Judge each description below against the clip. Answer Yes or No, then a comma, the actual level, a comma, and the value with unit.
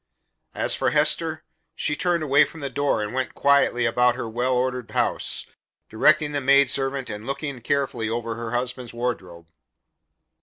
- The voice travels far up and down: No, average, 3.0 semitones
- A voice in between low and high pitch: No, low, 125 Hz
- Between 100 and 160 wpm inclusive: Yes, average, 155 wpm